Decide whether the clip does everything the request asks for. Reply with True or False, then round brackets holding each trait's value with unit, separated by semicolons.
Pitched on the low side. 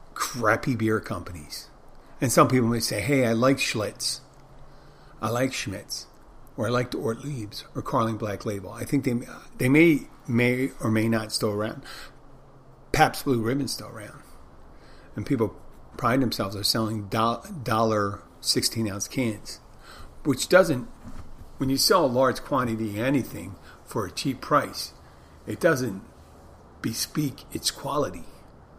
True (115 Hz)